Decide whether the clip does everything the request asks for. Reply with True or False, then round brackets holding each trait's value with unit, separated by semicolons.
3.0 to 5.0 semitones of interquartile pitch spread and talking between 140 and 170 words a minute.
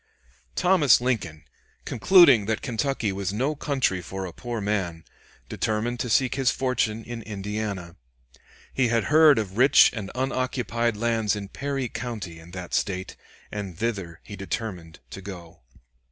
True (4.6 semitones; 145 wpm)